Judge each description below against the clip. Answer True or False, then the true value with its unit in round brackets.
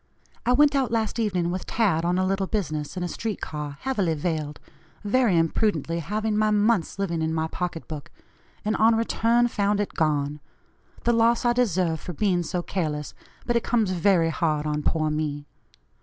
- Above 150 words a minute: True (185 wpm)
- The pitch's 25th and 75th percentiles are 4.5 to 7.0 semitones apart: True (5.5 semitones)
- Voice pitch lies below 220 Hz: True (185 Hz)